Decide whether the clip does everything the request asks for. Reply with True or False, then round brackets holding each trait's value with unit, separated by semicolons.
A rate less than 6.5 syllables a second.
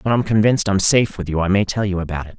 False (7.4 syllables/s)